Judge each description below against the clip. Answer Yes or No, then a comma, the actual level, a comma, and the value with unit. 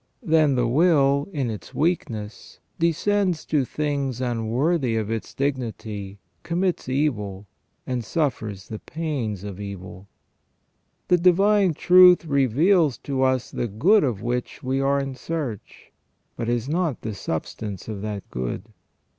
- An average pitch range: No, wide, 6.6 semitones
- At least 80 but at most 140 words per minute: Yes, slow, 135 wpm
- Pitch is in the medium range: No, low, 130 Hz